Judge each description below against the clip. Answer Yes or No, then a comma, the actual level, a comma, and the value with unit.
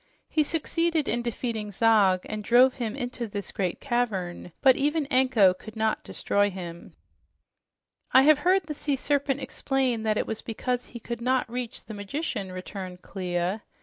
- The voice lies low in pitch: No, high, 235 Hz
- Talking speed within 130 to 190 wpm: Yes, average, 165 wpm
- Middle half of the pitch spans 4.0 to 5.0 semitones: Yes, average, 4.7 semitones